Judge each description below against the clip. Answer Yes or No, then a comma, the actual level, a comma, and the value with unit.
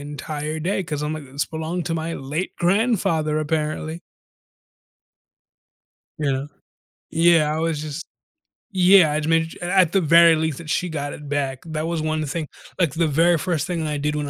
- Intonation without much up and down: Yes, narrow, 2.1 semitones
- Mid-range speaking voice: Yes, medium, 155 Hz